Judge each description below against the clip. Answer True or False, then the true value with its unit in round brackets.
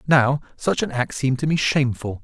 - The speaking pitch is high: False (135 Hz)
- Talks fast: True (215 wpm)